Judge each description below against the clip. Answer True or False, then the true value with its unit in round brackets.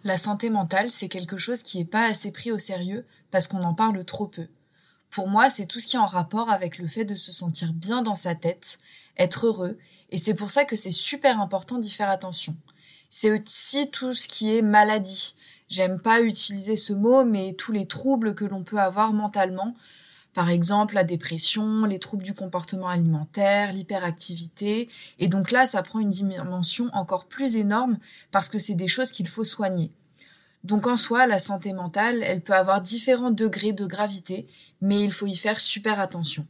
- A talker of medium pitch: False (200 Hz)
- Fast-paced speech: False (195 wpm)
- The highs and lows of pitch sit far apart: False (3.1 semitones)